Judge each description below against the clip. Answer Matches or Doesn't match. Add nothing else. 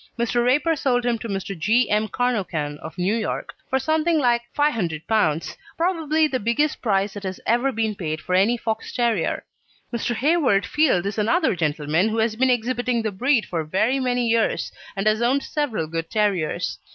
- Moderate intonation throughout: Matches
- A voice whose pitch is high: Matches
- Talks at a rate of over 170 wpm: Matches